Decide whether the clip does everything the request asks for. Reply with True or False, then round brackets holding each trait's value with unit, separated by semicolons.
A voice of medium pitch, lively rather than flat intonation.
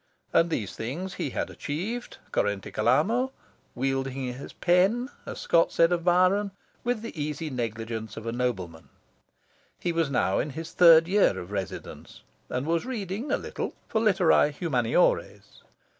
True (160 Hz; 7.0 semitones)